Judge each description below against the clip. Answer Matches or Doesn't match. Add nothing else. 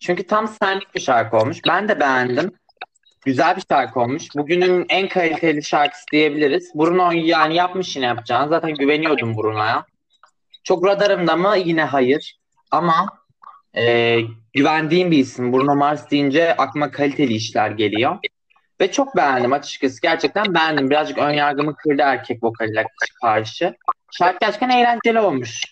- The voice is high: Doesn't match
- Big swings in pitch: Doesn't match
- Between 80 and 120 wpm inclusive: Doesn't match